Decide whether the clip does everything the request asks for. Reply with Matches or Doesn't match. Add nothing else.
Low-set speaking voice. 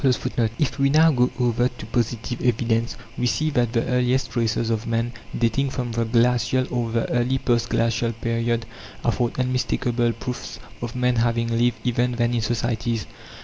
Matches